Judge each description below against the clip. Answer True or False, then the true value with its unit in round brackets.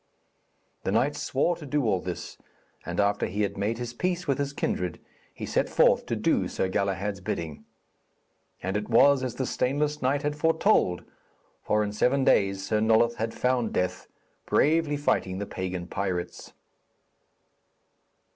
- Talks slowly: False (155 wpm)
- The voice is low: True (110 Hz)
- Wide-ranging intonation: True (6.4 semitones)